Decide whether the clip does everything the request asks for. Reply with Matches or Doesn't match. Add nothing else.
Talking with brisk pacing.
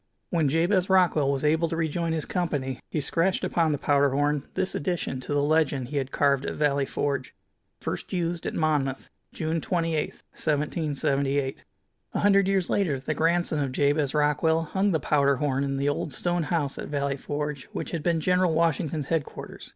Doesn't match